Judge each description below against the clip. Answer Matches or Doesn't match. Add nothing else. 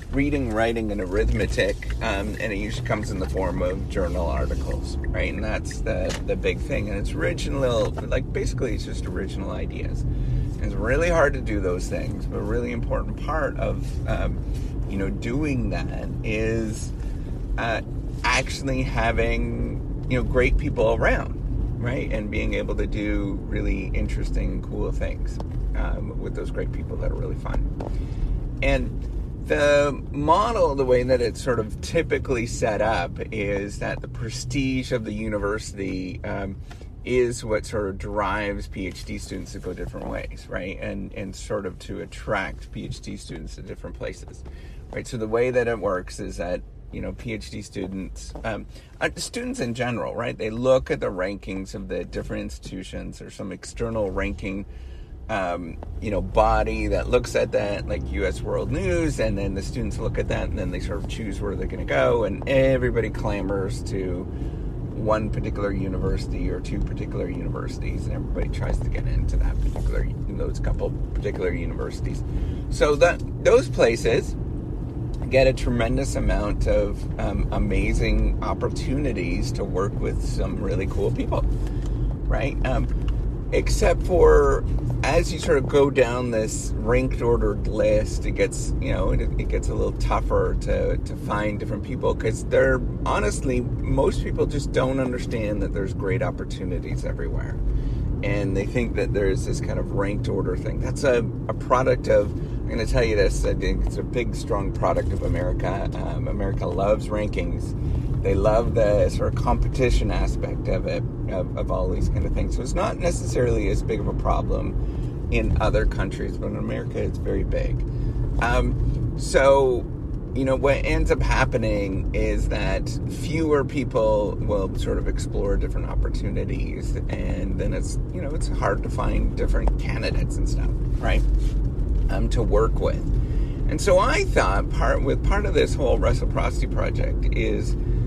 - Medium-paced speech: Matches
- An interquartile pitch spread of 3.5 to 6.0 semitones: Matches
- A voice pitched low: Matches